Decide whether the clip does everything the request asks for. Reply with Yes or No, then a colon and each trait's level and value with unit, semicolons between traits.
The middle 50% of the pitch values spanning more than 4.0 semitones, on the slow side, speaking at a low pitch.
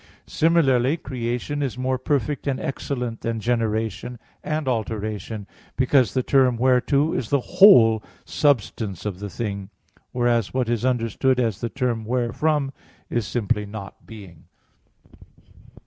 No: average, 3.2 semitones; slow, 130 wpm; low, 120 Hz